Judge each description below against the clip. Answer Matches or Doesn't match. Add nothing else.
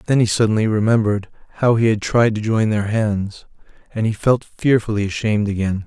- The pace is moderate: Matches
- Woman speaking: Doesn't match